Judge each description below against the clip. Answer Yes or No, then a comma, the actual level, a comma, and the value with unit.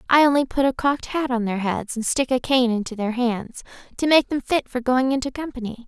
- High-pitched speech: Yes, very high, 250 Hz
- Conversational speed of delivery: No, fast, 235 wpm